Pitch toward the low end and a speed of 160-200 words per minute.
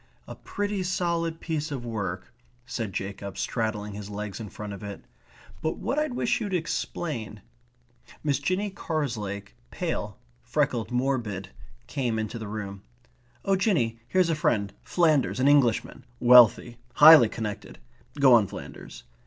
No: low, 120 Hz; average, 145 wpm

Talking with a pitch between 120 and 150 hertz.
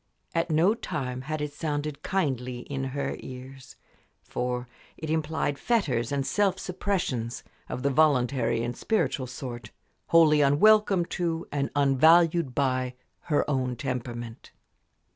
Yes: medium, 140 Hz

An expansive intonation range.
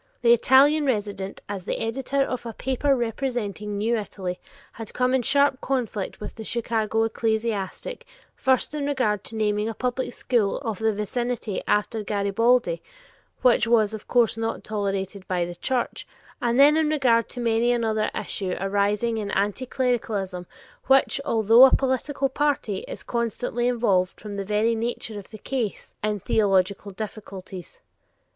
No: average, 3.5 semitones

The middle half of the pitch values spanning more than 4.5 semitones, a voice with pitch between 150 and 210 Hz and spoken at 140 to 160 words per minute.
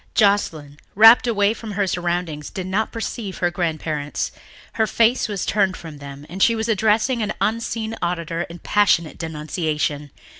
Yes: average, 5.3 semitones; medium, 185 Hz; average, 155 wpm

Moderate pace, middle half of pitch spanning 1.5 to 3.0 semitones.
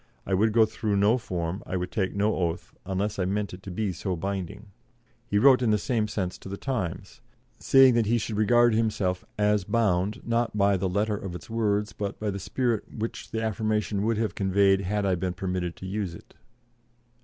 No: fast, 210 wpm; narrow, 2.6 semitones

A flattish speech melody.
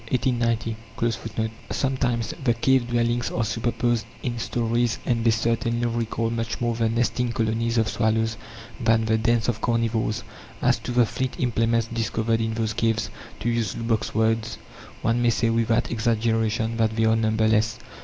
Yes: narrow, 0.9 semitones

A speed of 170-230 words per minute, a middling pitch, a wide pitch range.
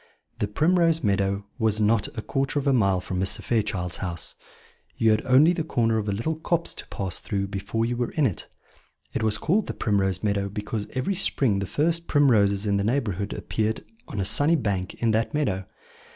No: average, 200 wpm; low, 110 Hz; wide, 5.7 semitones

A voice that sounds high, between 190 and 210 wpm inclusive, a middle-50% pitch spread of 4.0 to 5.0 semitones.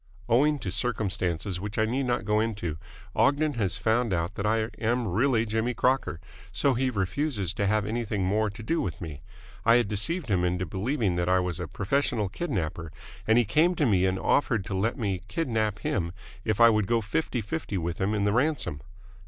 No: low, 110 Hz; average, 200 wpm; average, 4.3 semitones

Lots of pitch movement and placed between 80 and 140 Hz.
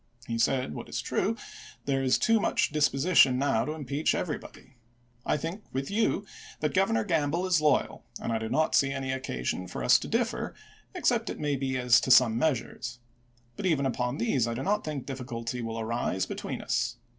No: average, 4.2 semitones; low, 135 Hz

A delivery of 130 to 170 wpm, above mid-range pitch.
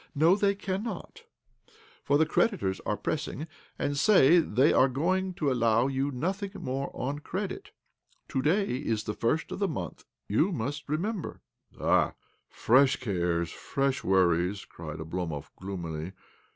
No: average, 155 wpm; medium, 140 Hz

